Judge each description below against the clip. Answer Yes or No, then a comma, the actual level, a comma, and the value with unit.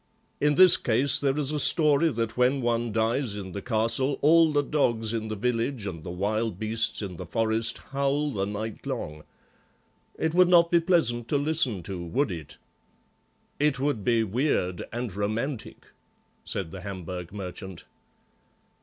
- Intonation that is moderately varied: No, wide, 5.8 semitones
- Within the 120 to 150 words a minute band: No, average, 165 wpm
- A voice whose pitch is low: Yes, low, 115 Hz